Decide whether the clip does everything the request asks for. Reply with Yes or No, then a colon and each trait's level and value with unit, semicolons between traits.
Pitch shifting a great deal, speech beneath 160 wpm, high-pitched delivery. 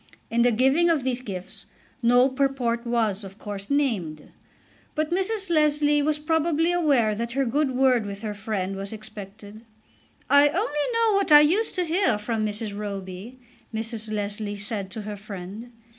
No: wide, 6.0 semitones; average, 165 wpm; high, 235 Hz